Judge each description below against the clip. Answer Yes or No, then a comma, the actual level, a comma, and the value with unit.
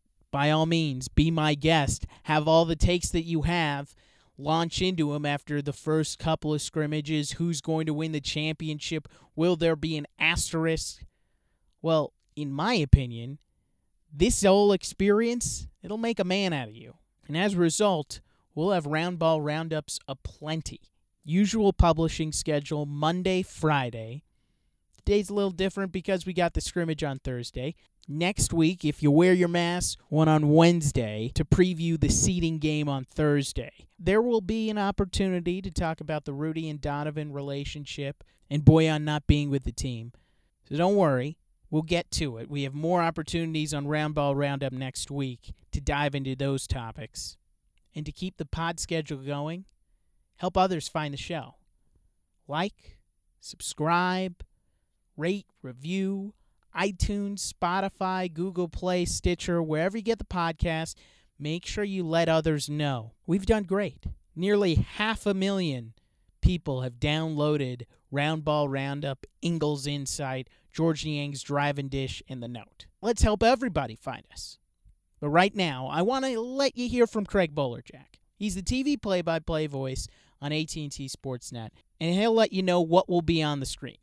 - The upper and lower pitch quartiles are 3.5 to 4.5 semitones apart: Yes, average, 4.0 semitones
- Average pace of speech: Yes, average, 160 wpm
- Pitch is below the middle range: No, medium, 155 Hz